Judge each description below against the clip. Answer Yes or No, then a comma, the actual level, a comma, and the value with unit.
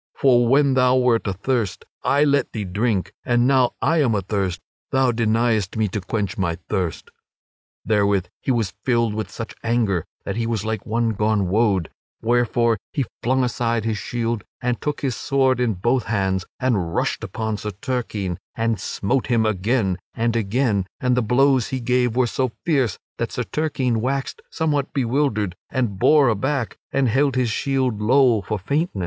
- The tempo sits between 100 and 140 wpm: No, average, 175 wpm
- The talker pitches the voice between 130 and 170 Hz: No, low, 115 Hz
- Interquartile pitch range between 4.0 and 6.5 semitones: No, average, 3.6 semitones